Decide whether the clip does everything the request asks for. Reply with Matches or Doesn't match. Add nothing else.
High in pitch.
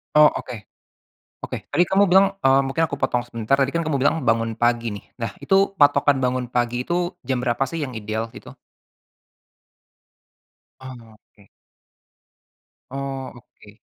Doesn't match